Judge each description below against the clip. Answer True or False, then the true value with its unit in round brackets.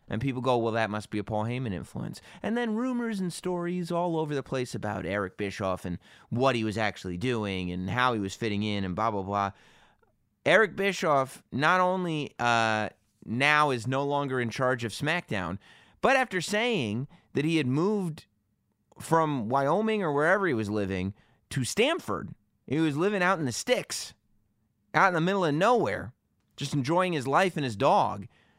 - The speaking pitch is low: True (130 Hz)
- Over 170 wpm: True (185 wpm)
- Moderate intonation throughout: False (8.3 semitones)